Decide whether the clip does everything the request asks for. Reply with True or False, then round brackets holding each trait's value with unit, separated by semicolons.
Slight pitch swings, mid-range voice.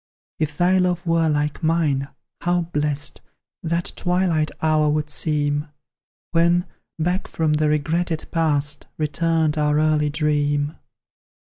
True (2.1 semitones; 155 Hz)